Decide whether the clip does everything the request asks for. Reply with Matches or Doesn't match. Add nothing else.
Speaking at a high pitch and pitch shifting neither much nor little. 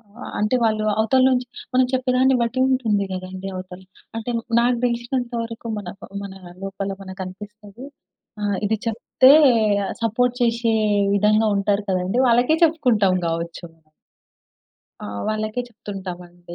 Matches